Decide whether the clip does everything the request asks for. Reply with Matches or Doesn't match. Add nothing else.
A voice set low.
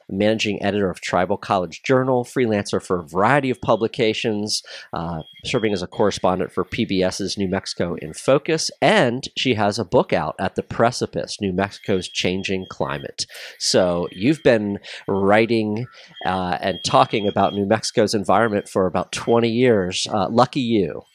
Matches